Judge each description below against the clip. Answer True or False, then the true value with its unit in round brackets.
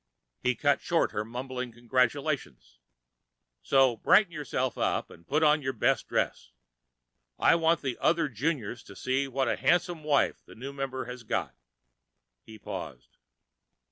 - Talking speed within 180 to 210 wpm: False (145 wpm)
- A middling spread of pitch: True (4.1 semitones)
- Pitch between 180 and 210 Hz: False (130 Hz)